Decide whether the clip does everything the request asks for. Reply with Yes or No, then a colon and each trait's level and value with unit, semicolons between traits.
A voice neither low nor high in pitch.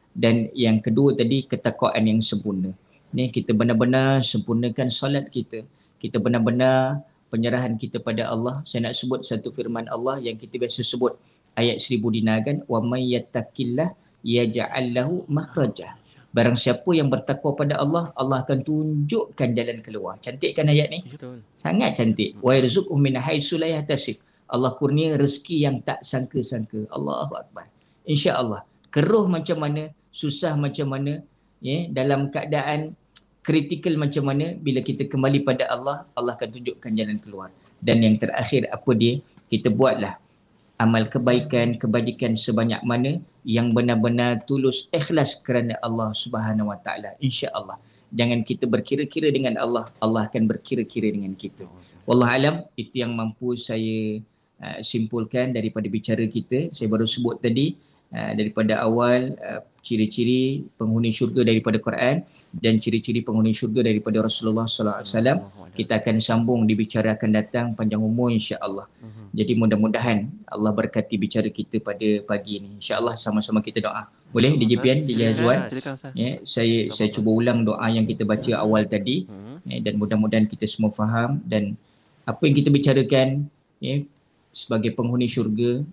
No: low, 120 Hz